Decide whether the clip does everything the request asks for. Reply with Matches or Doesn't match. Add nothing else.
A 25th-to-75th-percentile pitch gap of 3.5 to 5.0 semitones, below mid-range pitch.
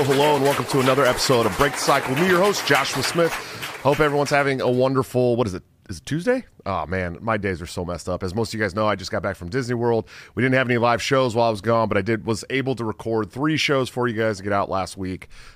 Matches